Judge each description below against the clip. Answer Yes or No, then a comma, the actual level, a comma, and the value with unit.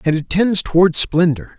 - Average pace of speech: Yes, average, 190 wpm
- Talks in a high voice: No, medium, 170 Hz